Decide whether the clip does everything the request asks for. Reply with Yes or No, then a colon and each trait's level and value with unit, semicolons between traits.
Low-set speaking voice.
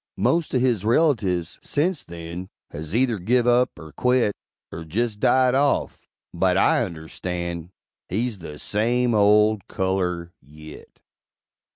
Yes: low, 105 Hz